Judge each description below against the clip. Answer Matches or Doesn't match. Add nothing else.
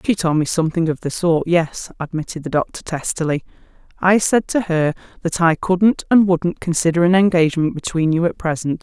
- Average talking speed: Matches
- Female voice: Matches